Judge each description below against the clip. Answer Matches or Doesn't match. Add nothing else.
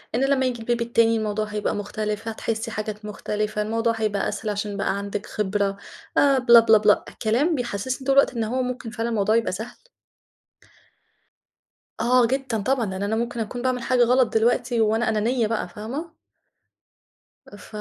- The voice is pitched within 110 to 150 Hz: Doesn't match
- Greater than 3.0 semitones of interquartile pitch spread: Doesn't match